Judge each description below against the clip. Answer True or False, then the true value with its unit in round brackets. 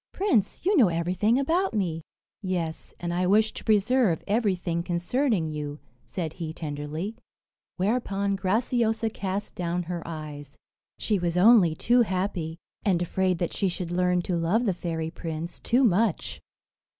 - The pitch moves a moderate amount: True (4.4 semitones)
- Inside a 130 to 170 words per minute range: True (150 wpm)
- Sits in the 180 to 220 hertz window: True (185 Hz)